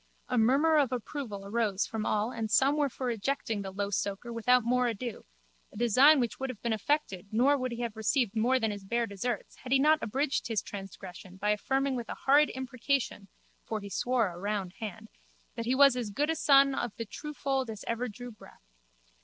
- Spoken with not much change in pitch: No, average, 4.2 semitones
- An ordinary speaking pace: No, fast, 210 wpm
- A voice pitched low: No, high, 235 Hz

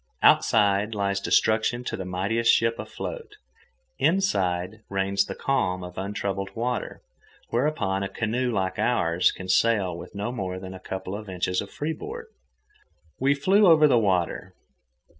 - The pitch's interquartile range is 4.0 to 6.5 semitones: Yes, average, 4.7 semitones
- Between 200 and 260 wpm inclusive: No, average, 150 wpm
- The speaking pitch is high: No, low, 100 Hz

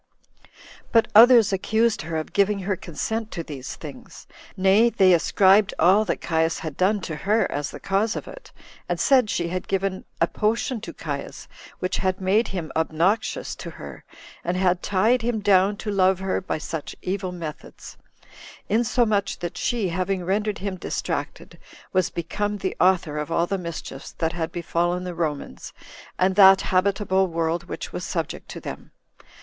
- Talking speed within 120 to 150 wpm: No, average, 170 wpm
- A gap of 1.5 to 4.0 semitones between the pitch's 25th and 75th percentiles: Yes, average, 3.2 semitones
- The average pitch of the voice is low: No, high, 190 Hz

